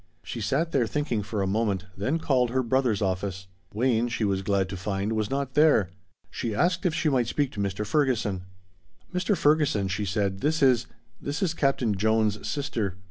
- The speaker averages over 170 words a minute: Yes, average, 190 wpm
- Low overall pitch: Yes, low, 115 Hz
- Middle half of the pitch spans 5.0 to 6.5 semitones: Yes, wide, 5.6 semitones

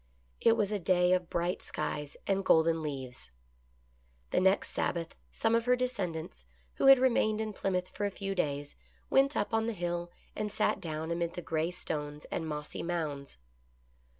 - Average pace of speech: Yes, average, 175 wpm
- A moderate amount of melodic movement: Yes, average, 4.7 semitones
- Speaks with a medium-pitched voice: Yes, medium, 175 Hz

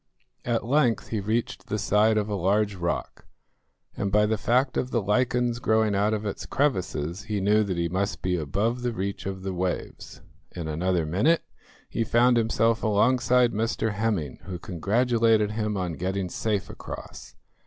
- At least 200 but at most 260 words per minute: No, average, 170 wpm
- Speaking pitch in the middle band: No, low, 105 Hz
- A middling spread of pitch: Yes, average, 3.5 semitones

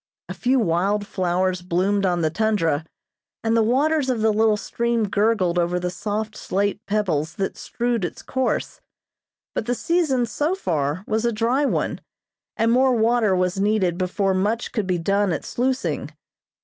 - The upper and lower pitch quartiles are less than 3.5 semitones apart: No, average, 4.4 semitones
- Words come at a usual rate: Yes, average, 165 wpm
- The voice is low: No, high, 210 Hz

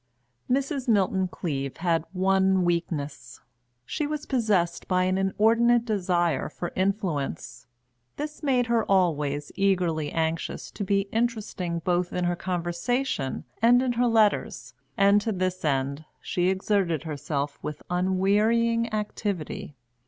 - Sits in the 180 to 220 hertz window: Yes, medium, 185 Hz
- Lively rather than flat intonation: No, average, 4.8 semitones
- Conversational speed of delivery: No, slow, 125 wpm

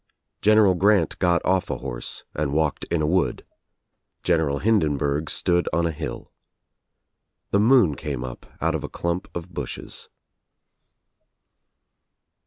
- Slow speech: Yes, slow, 130 wpm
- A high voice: No, very low, 85 Hz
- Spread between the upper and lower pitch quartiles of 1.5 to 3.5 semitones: No, average, 4.1 semitones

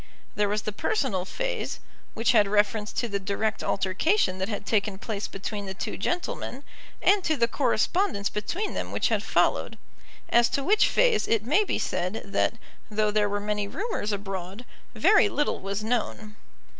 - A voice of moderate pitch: No, high, 215 Hz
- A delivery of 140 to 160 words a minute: No, average, 170 wpm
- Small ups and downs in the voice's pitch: No, wide, 5.5 semitones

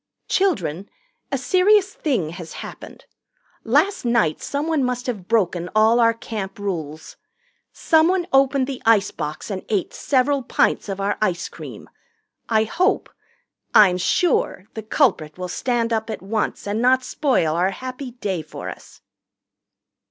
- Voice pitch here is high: Yes, high, 225 Hz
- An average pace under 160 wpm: Yes, average, 140 wpm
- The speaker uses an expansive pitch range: Yes, wide, 6.1 semitones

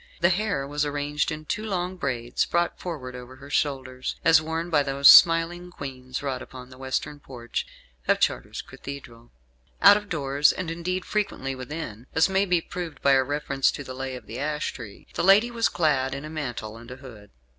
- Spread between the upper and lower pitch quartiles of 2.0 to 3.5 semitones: No, average, 4.4 semitones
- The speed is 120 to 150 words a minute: No, average, 200 wpm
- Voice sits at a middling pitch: Yes, medium, 145 Hz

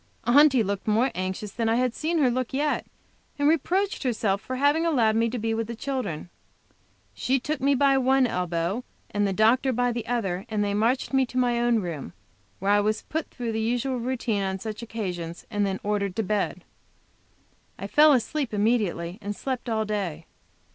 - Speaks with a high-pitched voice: Yes, high, 230 Hz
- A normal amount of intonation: Yes, average, 4.2 semitones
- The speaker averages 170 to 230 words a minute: Yes, average, 195 wpm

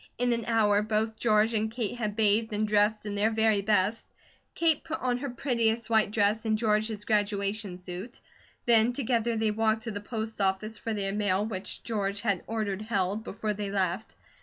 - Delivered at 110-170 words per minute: No, average, 190 wpm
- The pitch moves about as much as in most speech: No, narrow, 1.7 semitones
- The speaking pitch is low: No, high, 215 Hz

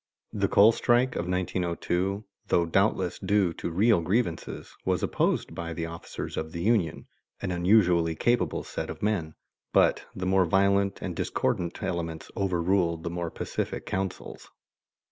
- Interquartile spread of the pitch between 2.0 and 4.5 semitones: Yes, average, 2.8 semitones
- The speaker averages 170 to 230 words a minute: No, average, 145 wpm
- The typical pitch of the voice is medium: No, very low, 90 Hz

